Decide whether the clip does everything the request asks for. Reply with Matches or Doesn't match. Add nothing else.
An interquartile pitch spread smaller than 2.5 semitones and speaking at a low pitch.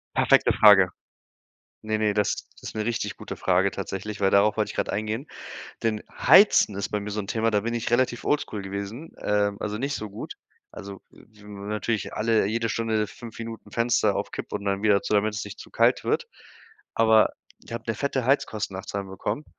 Matches